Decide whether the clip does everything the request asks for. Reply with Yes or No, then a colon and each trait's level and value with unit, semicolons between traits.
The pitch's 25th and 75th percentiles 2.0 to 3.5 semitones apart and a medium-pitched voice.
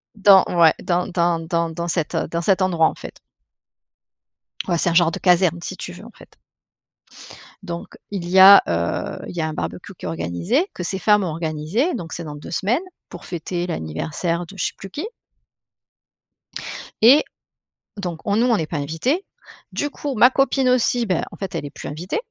No: average, 3.9 semitones; medium, 175 Hz